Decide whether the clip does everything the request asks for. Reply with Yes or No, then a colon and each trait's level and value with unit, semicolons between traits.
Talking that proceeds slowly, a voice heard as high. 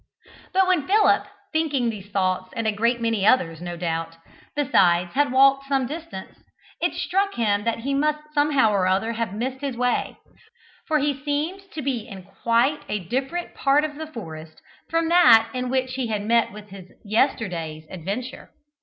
No: average, 175 wpm; high, 240 Hz